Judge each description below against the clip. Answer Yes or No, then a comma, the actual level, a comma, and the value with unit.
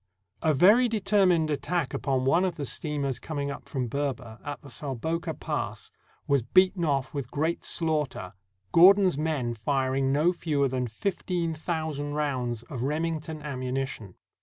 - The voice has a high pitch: No, medium, 145 Hz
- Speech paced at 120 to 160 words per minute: Yes, average, 150 wpm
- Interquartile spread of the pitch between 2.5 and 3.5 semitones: No, average, 3.9 semitones